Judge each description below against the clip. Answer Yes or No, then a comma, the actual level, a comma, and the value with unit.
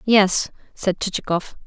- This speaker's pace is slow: Yes, slow, 110 wpm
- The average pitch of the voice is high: Yes, high, 195 Hz